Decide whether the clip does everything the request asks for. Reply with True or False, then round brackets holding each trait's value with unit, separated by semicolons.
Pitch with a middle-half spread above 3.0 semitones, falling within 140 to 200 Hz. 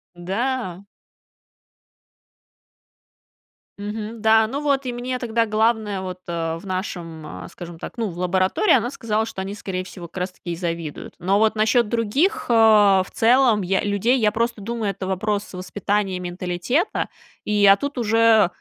False (3.8 semitones; 210 Hz)